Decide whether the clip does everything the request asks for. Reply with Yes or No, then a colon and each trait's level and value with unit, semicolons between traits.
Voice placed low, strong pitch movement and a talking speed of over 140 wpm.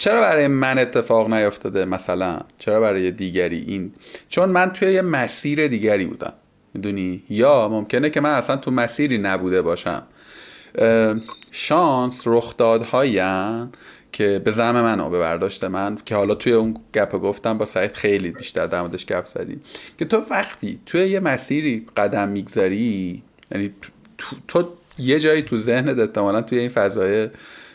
Yes: low, 115 Hz; wide, 6.2 semitones; average, 150 wpm